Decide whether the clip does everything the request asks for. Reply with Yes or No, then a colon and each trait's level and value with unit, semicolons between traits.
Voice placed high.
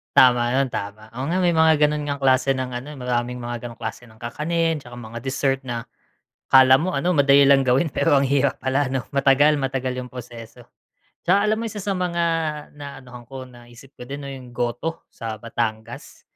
No: low, 135 Hz